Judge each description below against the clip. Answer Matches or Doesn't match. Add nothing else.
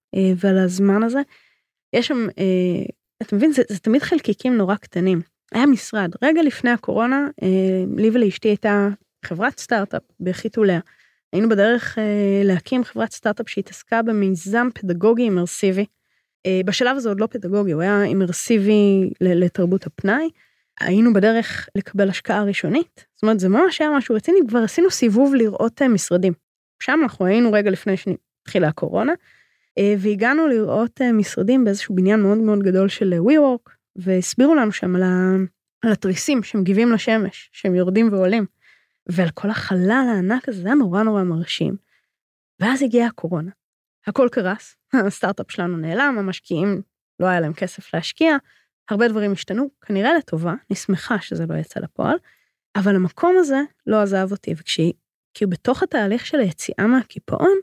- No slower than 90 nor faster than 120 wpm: Doesn't match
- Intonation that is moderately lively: Matches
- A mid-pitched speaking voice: Doesn't match